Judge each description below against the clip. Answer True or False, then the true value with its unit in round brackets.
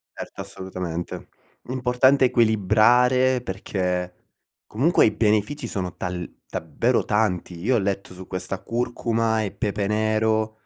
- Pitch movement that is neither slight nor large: True (4.4 semitones)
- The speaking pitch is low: True (110 Hz)